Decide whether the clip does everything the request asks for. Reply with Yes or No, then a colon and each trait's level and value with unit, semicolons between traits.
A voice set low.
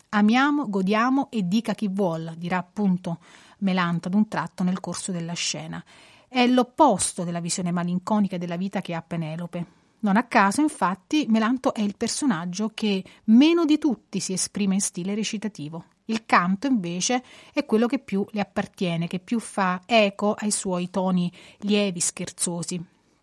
No: high, 200 Hz